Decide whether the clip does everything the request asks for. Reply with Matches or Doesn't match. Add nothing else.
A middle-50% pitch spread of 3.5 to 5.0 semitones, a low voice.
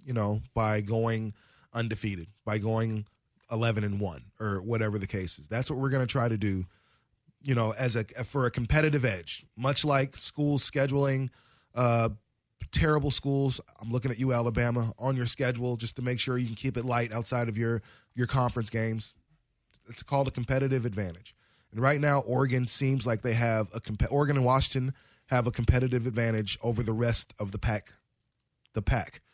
Doesn't match